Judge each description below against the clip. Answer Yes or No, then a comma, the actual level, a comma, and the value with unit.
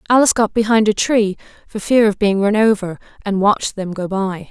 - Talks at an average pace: No, fast, 215 wpm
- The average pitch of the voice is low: No, high, 210 Hz